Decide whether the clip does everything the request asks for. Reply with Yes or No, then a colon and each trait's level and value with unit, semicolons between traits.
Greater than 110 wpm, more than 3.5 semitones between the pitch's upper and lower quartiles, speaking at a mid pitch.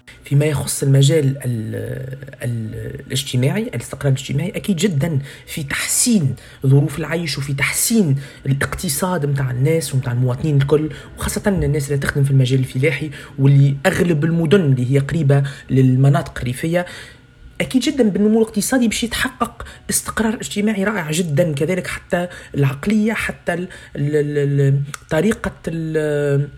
Yes: average, 125 wpm; average, 4.6 semitones; medium, 145 Hz